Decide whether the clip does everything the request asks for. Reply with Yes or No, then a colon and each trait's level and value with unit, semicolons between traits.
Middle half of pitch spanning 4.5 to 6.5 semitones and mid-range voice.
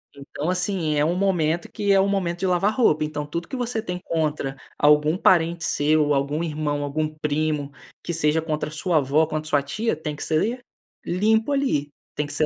No: average, 3.5 semitones; medium, 155 Hz